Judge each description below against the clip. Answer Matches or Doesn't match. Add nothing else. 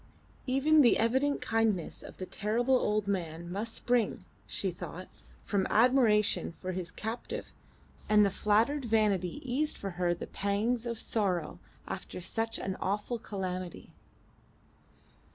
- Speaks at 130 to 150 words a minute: Matches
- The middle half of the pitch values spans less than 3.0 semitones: Doesn't match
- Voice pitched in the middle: Doesn't match